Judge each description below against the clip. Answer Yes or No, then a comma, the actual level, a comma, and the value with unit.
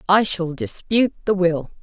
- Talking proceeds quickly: No, average, 165 wpm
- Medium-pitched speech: Yes, medium, 180 Hz